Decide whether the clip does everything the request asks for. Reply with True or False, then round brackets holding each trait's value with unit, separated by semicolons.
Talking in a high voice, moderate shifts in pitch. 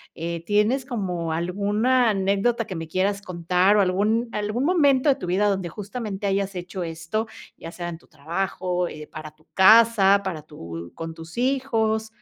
True (195 Hz; 4.4 semitones)